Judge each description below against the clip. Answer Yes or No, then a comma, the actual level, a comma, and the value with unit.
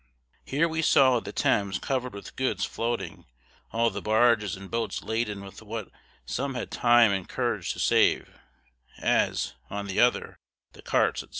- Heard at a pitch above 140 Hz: No, low, 115 Hz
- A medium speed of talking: Yes, average, 165 wpm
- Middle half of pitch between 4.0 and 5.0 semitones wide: No, average, 3.5 semitones